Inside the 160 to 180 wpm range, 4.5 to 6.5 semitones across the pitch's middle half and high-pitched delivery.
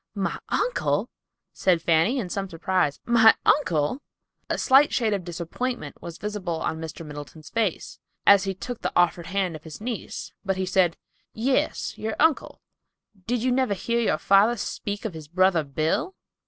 Yes: average, 170 wpm; wide, 5.6 semitones; high, 195 Hz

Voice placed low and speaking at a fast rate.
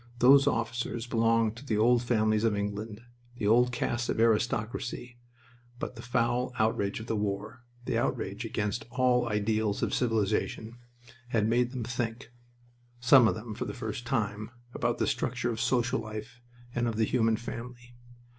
No: low, 115 Hz; average, 165 wpm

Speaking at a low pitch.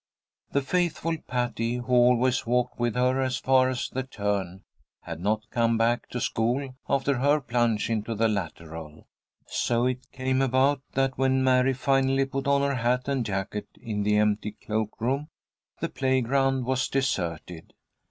Yes: low, 125 Hz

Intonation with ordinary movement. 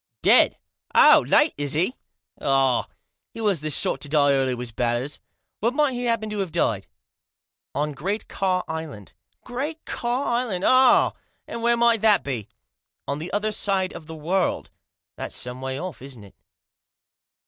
No: wide, 8.6 semitones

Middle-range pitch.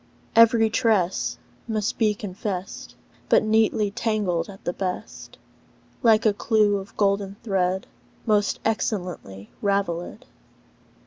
No: high, 205 Hz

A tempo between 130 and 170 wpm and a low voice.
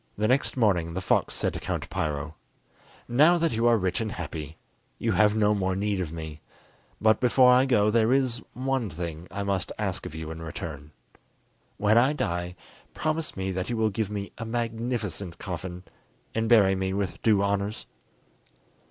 No: average, 180 wpm; low, 100 Hz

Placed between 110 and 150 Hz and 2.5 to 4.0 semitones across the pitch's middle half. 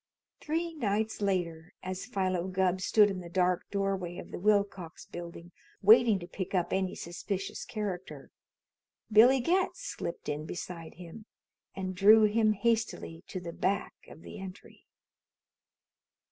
No: high, 190 Hz; average, 3.3 semitones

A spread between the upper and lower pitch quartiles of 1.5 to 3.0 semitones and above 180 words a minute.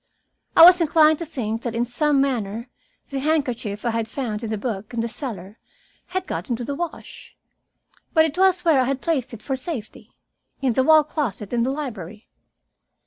No: average, 5.2 semitones; average, 195 wpm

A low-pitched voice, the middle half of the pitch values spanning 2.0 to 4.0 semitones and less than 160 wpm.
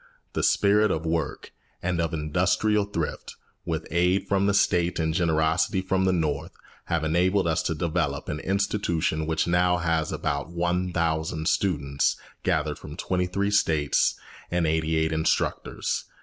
Yes: very low, 85 Hz; narrow, 2.6 semitones; average, 150 wpm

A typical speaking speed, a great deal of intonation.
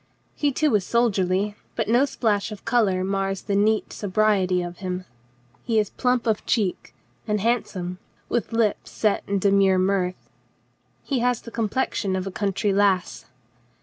No: average, 165 wpm; average, 3.2 semitones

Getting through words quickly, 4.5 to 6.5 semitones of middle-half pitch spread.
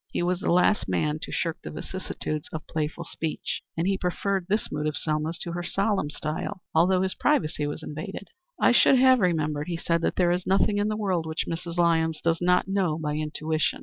No: fast, 215 wpm; average, 3.4 semitones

